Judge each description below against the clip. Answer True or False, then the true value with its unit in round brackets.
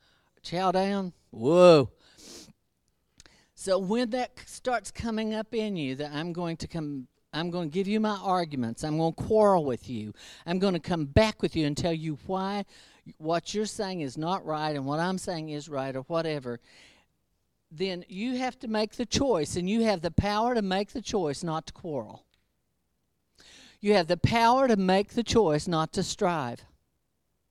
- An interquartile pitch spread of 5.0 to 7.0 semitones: True (5.3 semitones)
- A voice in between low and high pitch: True (180 Hz)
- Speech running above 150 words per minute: True (185 wpm)